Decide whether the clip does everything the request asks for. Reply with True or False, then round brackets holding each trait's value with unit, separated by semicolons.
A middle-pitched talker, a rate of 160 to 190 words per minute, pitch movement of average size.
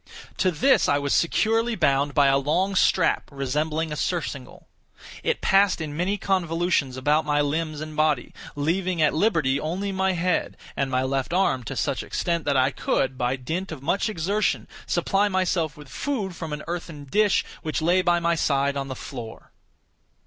True (160 Hz; 180 wpm; 4.7 semitones)